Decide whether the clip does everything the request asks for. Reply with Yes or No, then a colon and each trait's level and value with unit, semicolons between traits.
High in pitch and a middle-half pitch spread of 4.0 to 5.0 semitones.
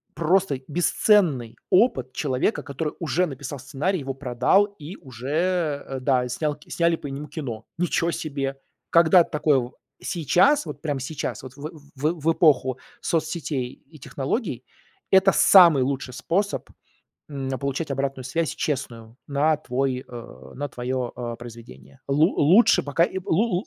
No: medium, 145 Hz; average, 4.3 semitones